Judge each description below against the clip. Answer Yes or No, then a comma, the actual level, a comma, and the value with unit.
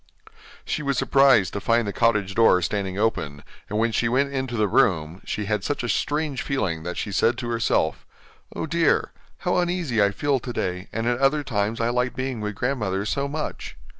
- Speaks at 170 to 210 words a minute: Yes, average, 195 wpm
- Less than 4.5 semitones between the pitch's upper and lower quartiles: No, average, 5.1 semitones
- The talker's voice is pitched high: No, low, 115 Hz